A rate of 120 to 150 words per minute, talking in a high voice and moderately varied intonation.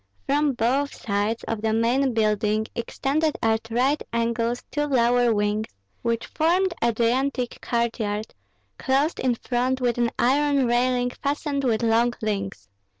Yes: average, 140 wpm; high, 240 Hz; average, 3.1 semitones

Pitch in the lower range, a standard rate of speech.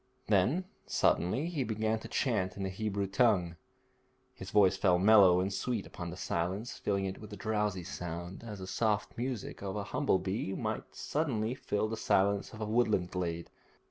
Yes: low, 100 Hz; average, 175 wpm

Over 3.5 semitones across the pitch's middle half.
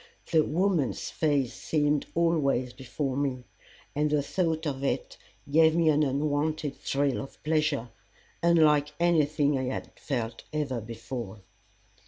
No: average, 2.9 semitones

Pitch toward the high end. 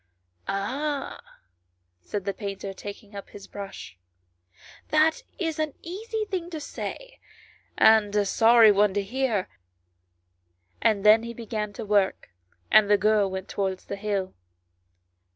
Yes: high, 210 Hz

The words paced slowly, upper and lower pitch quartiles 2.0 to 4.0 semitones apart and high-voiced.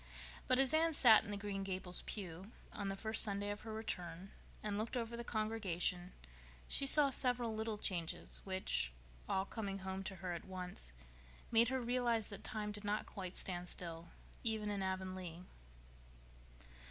No: average, 165 wpm; average, 3.2 semitones; high, 205 Hz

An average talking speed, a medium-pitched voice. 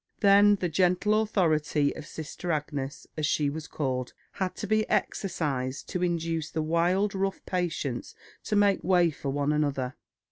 Yes: average, 155 wpm; medium, 165 Hz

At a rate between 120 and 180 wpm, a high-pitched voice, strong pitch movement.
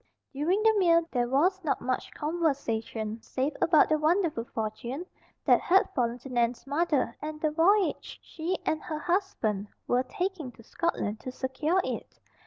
Yes: average, 160 wpm; very high, 300 Hz; wide, 5.8 semitones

